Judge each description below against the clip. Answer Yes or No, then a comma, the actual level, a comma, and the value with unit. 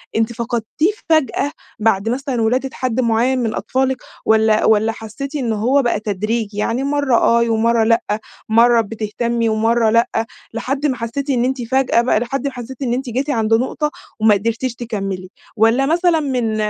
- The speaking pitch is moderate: No, high, 235 Hz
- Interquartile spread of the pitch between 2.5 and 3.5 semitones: Yes, average, 3.0 semitones